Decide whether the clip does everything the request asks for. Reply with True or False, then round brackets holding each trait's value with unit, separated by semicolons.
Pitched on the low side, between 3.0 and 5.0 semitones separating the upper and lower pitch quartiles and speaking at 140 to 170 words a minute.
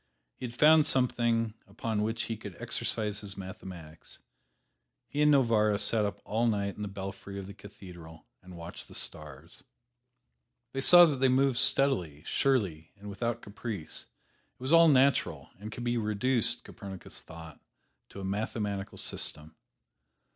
True (105 Hz; 4.1 semitones; 155 wpm)